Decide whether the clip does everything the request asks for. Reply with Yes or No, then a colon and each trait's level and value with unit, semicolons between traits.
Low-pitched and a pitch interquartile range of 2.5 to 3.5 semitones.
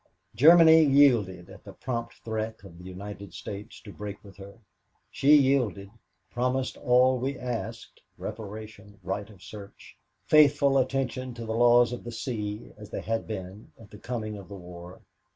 No: low, 110 Hz; average, 4.1 semitones